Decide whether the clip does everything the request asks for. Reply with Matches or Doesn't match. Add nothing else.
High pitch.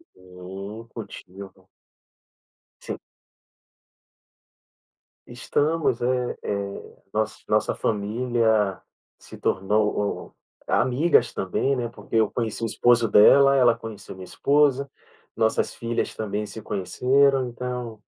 Doesn't match